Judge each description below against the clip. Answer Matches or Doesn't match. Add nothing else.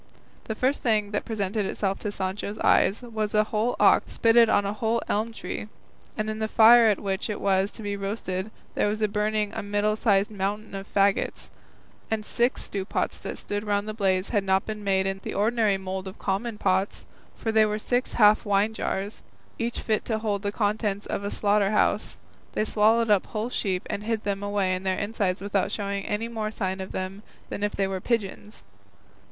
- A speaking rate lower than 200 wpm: Doesn't match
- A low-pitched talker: Doesn't match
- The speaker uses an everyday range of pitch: Doesn't match